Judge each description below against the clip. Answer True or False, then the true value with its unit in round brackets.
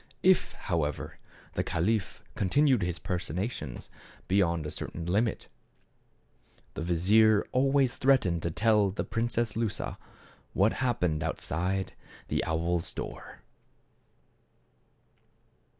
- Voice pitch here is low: True (95 Hz)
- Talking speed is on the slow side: True (100 wpm)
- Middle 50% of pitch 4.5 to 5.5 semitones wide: True (5.1 semitones)